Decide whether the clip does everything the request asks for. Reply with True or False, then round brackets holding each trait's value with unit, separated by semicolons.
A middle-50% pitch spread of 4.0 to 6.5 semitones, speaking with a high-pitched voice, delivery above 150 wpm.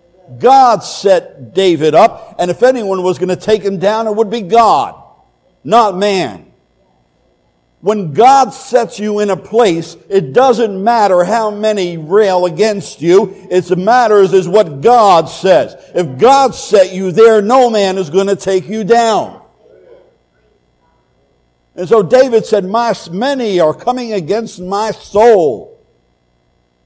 False (4.4 semitones; 195 Hz; 145 wpm)